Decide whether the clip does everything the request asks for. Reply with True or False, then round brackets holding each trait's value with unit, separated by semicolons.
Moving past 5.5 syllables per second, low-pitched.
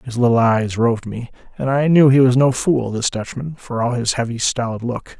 False (5.2 syllables/s; 125 Hz)